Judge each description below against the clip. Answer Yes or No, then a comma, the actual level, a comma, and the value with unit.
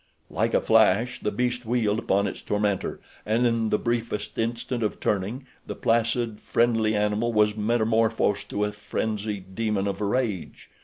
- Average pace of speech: Yes, average, 155 wpm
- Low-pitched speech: Yes, low, 110 Hz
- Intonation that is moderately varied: No, narrow, 2.1 semitones